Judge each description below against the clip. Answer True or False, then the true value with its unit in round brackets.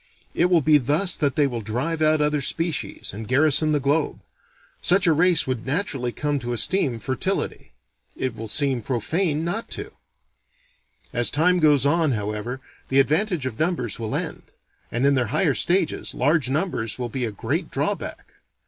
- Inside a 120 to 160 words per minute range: False (170 wpm)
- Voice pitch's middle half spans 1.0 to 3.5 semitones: False (4.8 semitones)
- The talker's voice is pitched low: False (145 Hz)